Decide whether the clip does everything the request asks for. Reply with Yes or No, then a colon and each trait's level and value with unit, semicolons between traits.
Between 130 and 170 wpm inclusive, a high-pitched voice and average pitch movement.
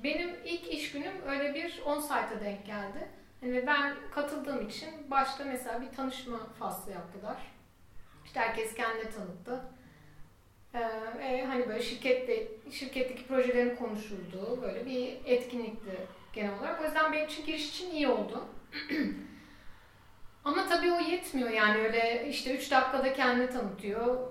Yes: fast, 140 wpm; very high, 255 Hz; average, 4.1 semitones